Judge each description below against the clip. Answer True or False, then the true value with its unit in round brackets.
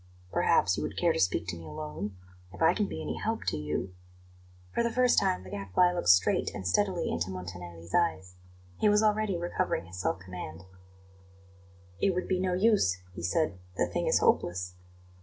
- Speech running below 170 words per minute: False (195 wpm)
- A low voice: True (90 Hz)